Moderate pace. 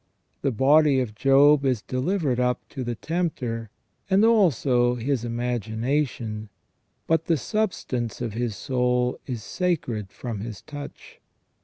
No: slow, 130 wpm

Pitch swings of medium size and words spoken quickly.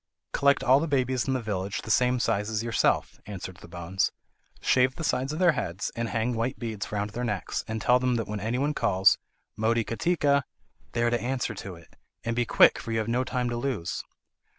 Yes: average, 3.4 semitones; fast, 215 wpm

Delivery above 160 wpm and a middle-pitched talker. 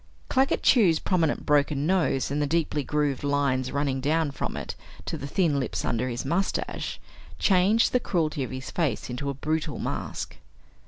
Yes: average, 170 wpm; medium, 145 Hz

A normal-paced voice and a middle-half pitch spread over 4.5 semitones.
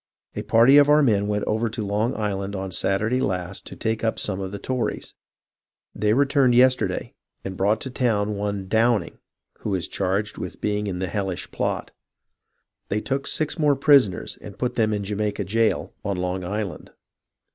No: average, 180 wpm; average, 3.5 semitones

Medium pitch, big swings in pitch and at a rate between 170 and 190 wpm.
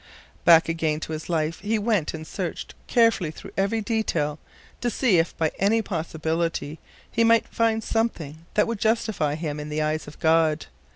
Yes: medium, 165 Hz; wide, 5.9 semitones; average, 175 wpm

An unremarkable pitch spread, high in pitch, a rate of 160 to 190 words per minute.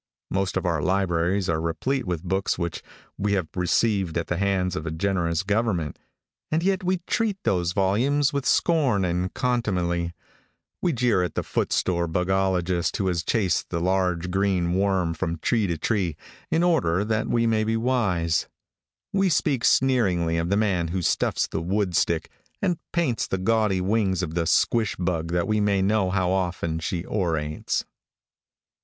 No: average, 4.2 semitones; very low, 95 Hz; average, 165 wpm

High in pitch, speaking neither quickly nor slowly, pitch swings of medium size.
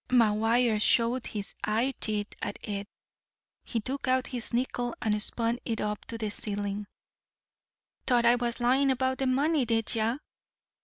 Yes: high, 235 Hz; average, 150 wpm; average, 3.0 semitones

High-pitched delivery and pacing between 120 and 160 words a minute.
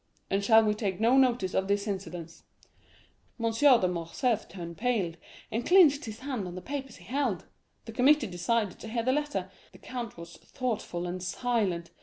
No: high, 220 Hz; average, 180 wpm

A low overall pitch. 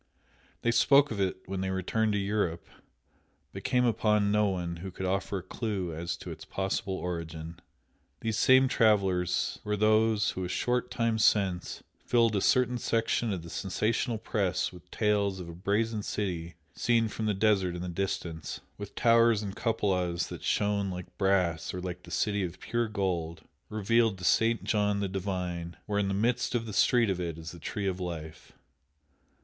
Yes: low, 100 Hz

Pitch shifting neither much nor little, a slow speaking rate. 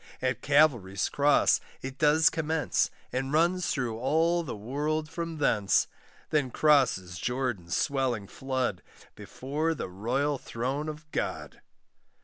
Yes: average, 4.2 semitones; slow, 125 wpm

